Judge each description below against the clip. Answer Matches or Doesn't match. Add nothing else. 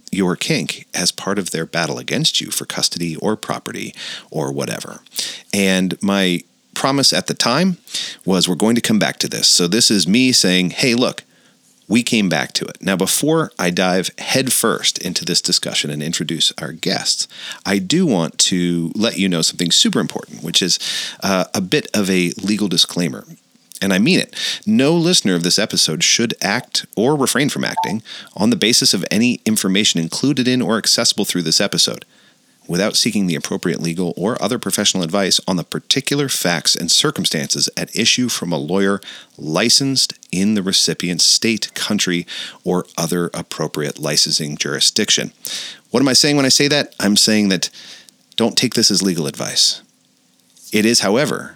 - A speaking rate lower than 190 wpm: Matches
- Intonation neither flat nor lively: Doesn't match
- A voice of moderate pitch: Doesn't match